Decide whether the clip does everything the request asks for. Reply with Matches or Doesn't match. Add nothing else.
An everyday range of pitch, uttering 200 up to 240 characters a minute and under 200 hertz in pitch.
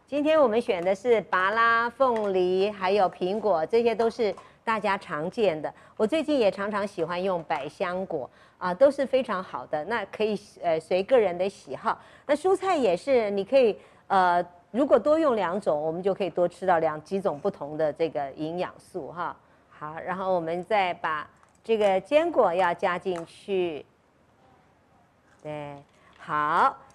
Matches